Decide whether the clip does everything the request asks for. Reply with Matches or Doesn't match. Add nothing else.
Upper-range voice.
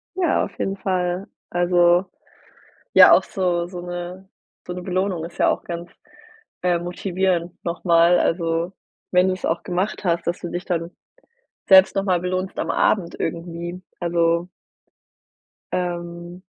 Doesn't match